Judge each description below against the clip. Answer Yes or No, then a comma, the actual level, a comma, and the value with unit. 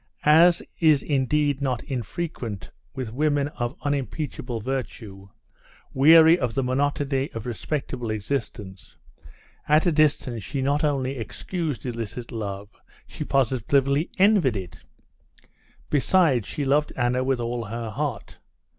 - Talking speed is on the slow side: Yes, slow, 120 wpm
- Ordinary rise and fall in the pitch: Yes, average, 4.0 semitones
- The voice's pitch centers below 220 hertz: Yes, low, 135 Hz